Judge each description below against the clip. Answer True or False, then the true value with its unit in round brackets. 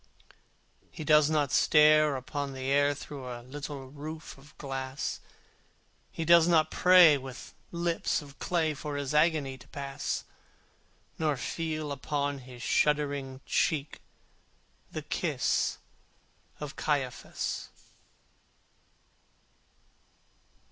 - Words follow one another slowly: True (105 wpm)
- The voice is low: False (145 Hz)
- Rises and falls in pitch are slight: True (2.2 semitones)